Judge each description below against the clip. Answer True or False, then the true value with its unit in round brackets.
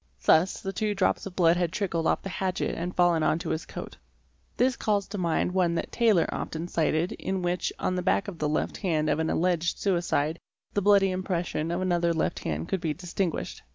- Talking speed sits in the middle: False (215 wpm)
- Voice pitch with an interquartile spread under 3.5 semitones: True (2.5 semitones)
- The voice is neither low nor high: True (175 Hz)